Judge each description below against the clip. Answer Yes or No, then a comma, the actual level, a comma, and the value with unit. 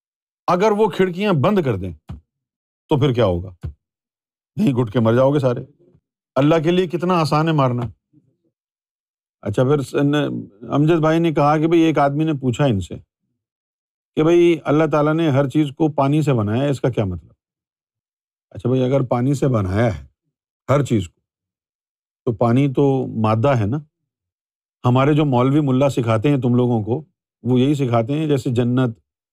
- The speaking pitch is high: No, medium, 140 Hz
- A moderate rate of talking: Yes, average, 170 wpm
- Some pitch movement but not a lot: Yes, average, 4.1 semitones